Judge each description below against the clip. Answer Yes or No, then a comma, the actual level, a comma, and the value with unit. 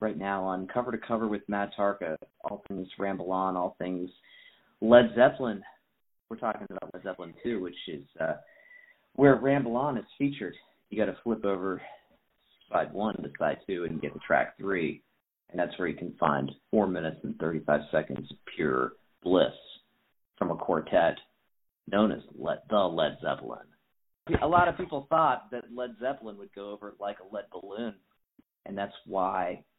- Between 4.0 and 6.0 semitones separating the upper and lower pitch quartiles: Yes, average, 4.5 semitones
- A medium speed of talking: Yes, average, 175 wpm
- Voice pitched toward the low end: Yes, low, 105 Hz